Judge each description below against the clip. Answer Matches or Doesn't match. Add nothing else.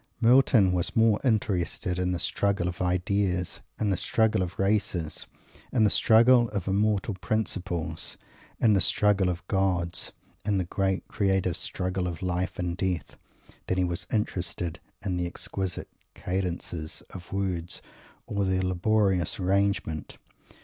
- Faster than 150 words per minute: Doesn't match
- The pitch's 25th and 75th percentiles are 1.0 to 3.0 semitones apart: Matches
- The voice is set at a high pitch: Doesn't match